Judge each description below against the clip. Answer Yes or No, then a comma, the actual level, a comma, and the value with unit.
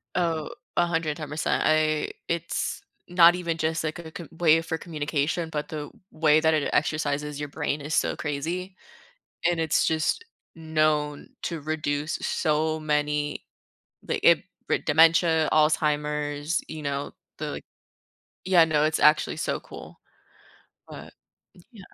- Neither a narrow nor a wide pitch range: No, narrow, 1.6 semitones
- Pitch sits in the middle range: Yes, medium, 155 Hz